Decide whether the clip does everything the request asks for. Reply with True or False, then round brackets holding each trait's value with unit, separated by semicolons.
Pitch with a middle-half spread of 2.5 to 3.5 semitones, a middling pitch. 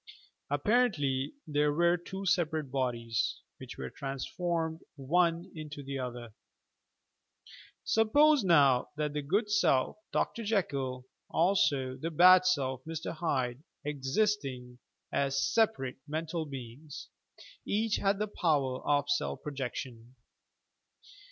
False (5.1 semitones; 150 Hz)